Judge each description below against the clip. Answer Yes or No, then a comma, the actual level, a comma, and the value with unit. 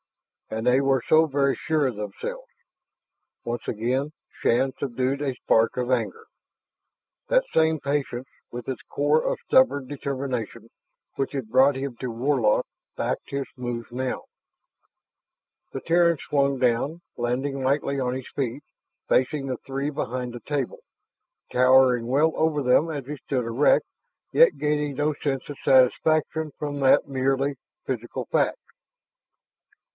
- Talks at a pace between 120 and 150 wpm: Yes, average, 140 wpm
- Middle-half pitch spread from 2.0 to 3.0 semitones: Yes, average, 2.7 semitones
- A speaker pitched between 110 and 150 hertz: Yes, low, 135 Hz